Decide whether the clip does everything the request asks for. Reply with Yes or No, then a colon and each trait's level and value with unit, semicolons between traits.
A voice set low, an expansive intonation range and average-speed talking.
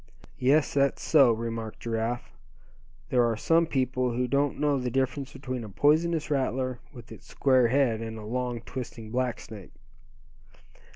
No: low, 125 Hz; average, 3.0 semitones; average, 155 wpm